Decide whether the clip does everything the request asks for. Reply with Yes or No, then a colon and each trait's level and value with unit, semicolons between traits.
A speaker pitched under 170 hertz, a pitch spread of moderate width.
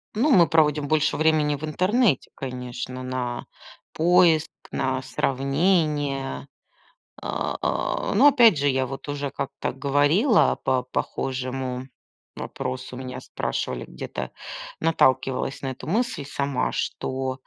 Yes: medium, 140 Hz; average, 3.2 semitones